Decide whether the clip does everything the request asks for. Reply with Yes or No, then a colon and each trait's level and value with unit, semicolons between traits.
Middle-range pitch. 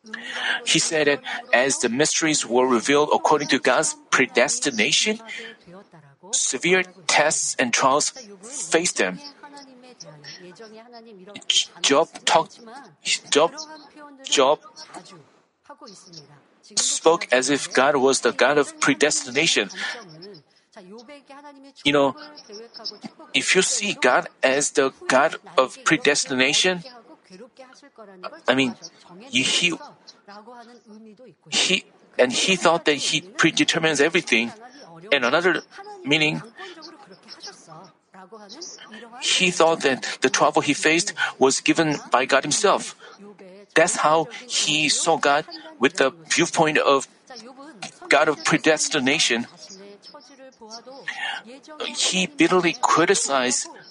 No: high, 195 Hz